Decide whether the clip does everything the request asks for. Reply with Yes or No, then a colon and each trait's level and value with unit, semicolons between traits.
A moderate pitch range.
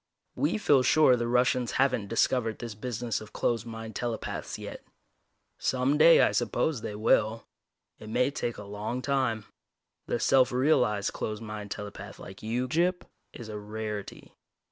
Yes: average, 3.0 semitones